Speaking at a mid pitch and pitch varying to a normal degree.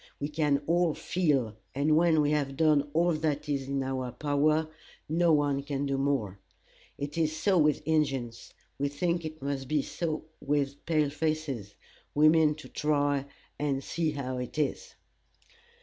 No: medium, 145 Hz; narrow, 2.1 semitones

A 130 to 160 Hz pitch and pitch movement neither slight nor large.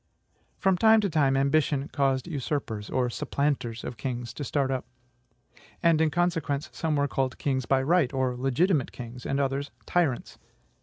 Yes: medium, 140 Hz; average, 3.2 semitones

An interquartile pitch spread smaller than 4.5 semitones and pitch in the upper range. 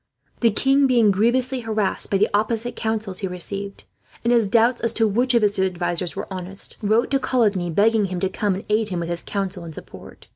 Yes: average, 3.5 semitones; high, 210 Hz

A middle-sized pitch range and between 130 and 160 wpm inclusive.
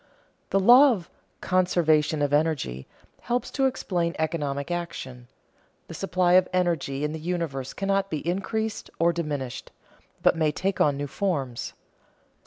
Yes: average, 4.1 semitones; average, 140 wpm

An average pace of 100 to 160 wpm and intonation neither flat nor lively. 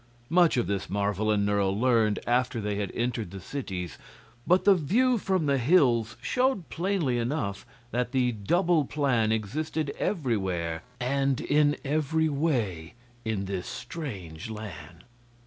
No: average, 140 wpm; wide, 7.0 semitones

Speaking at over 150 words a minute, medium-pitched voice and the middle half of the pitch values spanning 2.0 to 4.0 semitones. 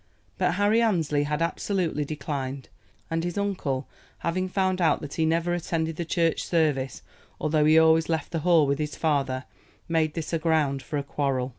Yes: average, 180 wpm; medium, 160 Hz; average, 2.7 semitones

